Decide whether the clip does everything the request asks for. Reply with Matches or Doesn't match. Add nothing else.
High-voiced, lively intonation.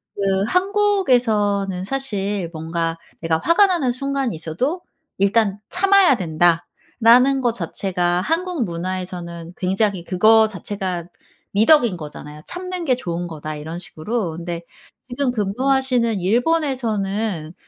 Matches